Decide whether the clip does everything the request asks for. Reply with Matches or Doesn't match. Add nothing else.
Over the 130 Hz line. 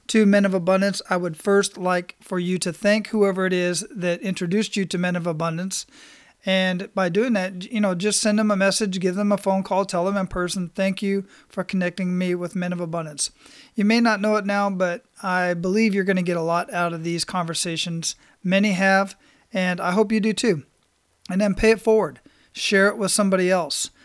Matches